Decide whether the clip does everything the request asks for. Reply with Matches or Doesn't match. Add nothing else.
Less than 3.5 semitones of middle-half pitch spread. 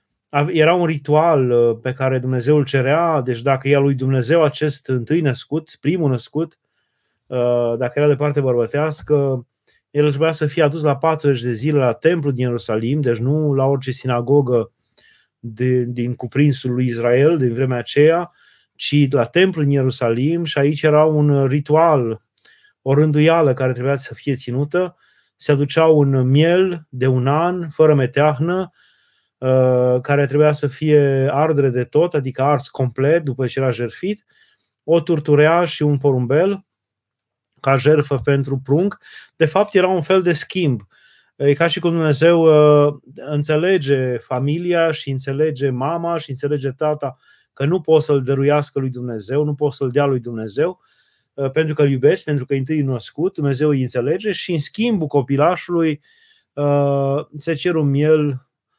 Matches